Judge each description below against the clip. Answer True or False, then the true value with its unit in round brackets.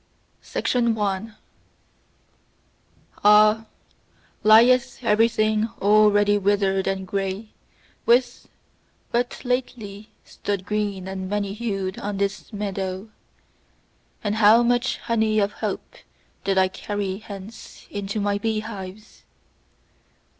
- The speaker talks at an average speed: False (95 wpm)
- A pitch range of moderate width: False (2.1 semitones)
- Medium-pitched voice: False (205 Hz)